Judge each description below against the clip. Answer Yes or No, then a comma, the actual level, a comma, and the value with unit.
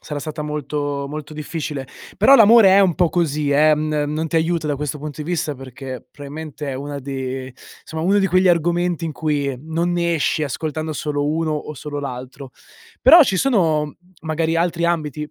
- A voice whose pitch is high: No, medium, 155 Hz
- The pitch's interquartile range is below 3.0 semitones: Yes, narrow, 2.6 semitones